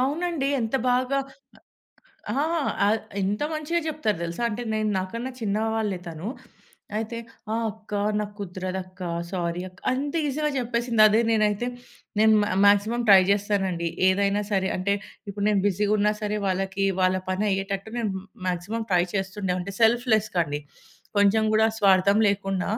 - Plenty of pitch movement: No, average, 2.8 semitones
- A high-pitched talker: Yes, high, 205 Hz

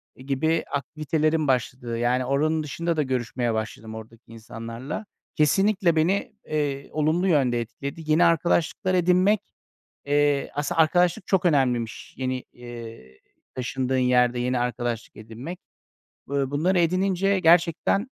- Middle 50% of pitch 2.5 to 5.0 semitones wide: No, wide, 5.4 semitones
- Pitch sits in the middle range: Yes, medium, 145 Hz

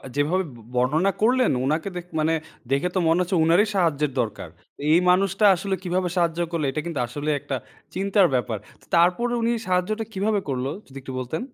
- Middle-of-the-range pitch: Yes, medium, 175 Hz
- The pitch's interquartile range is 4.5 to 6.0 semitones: Yes, average, 5.0 semitones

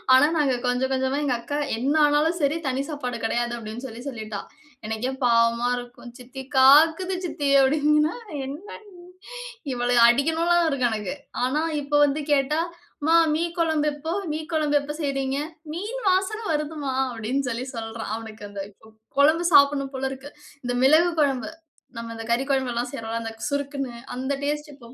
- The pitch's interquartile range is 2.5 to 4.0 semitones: Yes, average, 3.7 semitones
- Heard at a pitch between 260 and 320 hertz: Yes, very high, 275 Hz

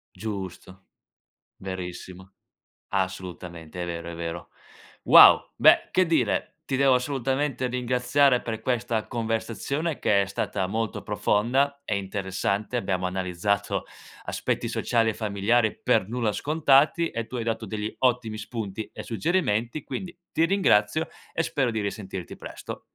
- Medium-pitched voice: No, low, 110 Hz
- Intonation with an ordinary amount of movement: Yes, average, 4.9 semitones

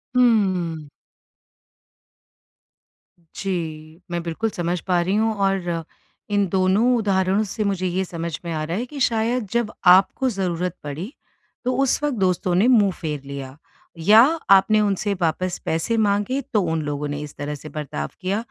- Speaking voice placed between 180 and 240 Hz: Yes, medium, 185 Hz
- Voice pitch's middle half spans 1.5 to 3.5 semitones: No, average, 4.5 semitones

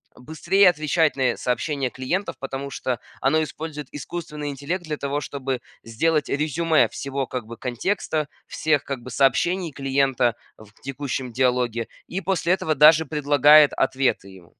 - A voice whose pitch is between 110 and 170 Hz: Yes, medium, 140 Hz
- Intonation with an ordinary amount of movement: Yes, average, 3.4 semitones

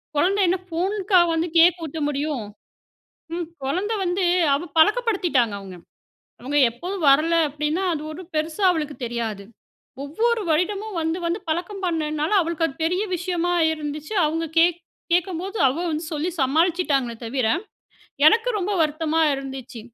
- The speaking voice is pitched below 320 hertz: No, very high, 325 Hz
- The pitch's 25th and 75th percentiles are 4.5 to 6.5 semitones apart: No, average, 3.7 semitones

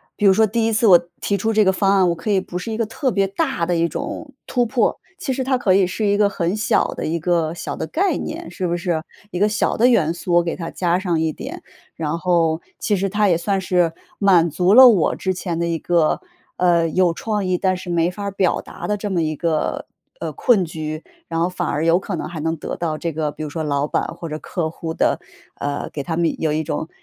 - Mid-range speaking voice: Yes, medium, 175 Hz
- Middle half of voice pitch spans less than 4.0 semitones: Yes, average, 3.5 semitones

